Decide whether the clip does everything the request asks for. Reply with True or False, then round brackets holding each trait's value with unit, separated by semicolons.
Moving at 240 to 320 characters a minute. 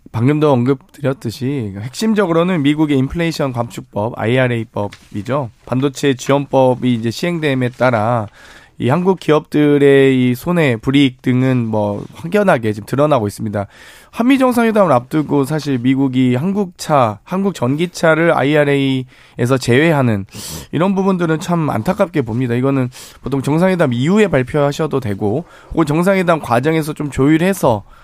False (340 characters per minute)